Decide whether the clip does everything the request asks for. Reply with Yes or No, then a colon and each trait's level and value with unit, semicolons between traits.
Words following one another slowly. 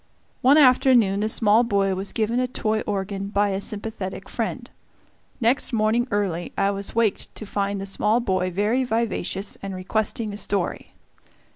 No: average, 160 wpm